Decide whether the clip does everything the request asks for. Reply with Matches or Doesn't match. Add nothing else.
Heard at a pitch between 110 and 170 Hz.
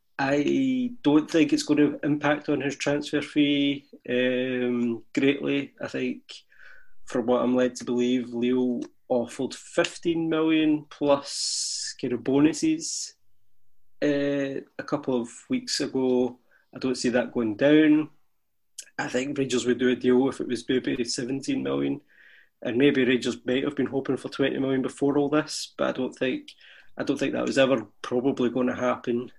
Matches